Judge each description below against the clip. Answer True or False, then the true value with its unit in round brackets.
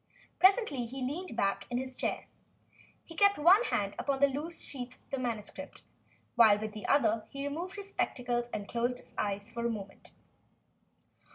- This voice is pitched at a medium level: False (250 Hz)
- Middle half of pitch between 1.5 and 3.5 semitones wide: False (4.9 semitones)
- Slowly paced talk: False (175 wpm)